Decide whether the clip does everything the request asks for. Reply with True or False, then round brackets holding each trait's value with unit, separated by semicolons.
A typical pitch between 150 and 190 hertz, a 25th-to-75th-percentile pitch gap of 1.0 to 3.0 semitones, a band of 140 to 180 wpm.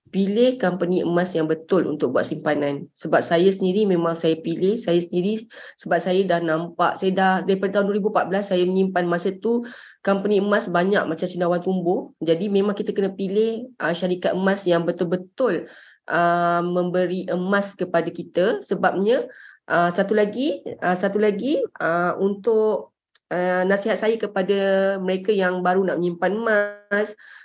True (185 Hz; 2.6 semitones; 150 wpm)